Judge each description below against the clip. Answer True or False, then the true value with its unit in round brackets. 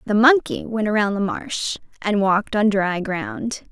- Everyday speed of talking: True (180 wpm)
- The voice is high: True (205 Hz)